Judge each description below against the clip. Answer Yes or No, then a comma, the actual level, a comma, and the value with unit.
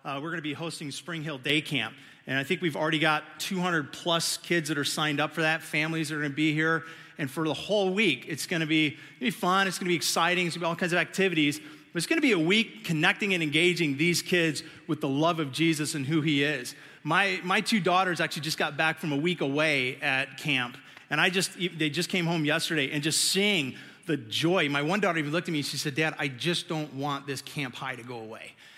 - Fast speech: Yes, fast, 260 wpm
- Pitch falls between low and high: Yes, medium, 160 Hz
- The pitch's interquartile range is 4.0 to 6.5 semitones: No, average, 2.7 semitones